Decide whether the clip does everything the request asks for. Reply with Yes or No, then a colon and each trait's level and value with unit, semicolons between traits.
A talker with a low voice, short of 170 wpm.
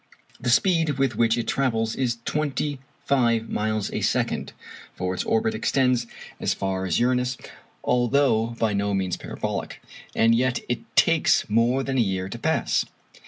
Yes: low, 120 Hz; average, 160 wpm